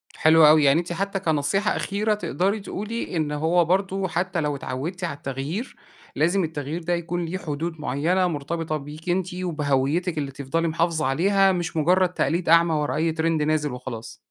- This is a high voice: No, medium, 165 Hz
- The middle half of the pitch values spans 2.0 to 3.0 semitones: No, average, 3.5 semitones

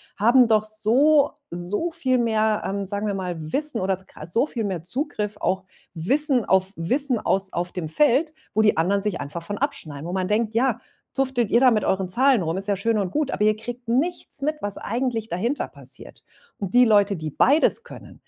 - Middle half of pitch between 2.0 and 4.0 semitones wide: No, average, 5.1 semitones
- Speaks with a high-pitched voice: Yes, high, 215 Hz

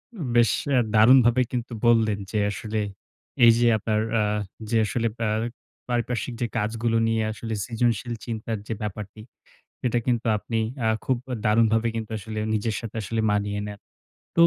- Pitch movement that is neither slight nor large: No, narrow, 1.8 semitones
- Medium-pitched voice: No, low, 115 Hz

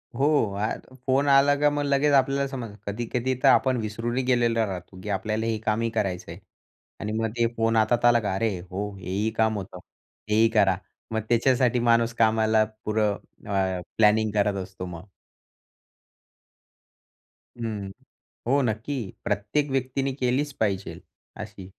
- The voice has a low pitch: Yes, low, 110 Hz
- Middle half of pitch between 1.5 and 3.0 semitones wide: No, average, 3.6 semitones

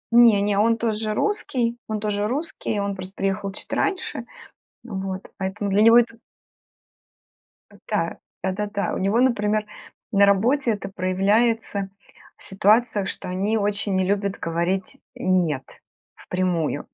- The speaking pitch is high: Yes, high, 205 Hz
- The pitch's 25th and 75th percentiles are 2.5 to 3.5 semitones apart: Yes, average, 2.8 semitones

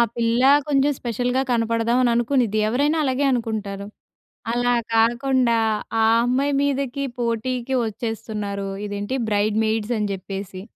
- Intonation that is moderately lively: Yes, average, 3.0 semitones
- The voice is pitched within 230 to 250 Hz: Yes, high, 235 Hz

